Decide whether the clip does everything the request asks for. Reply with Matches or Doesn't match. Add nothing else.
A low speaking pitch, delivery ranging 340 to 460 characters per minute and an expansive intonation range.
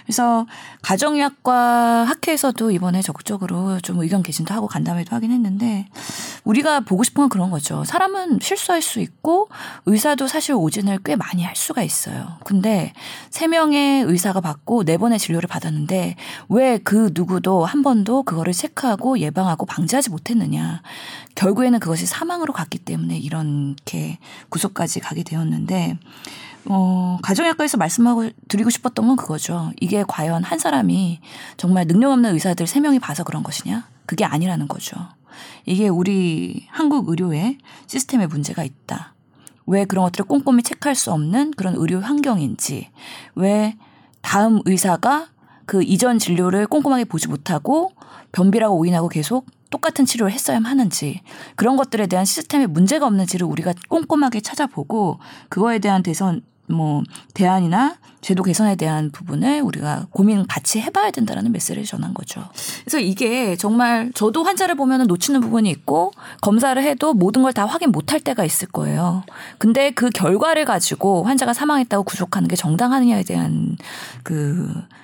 Doesn't match